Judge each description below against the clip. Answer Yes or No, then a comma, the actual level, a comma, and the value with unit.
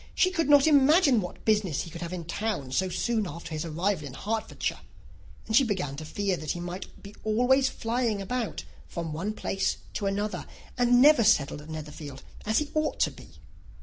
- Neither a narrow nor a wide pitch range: No, wide, 6.6 semitones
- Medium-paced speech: Yes, average, 195 wpm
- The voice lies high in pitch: Yes, high, 205 Hz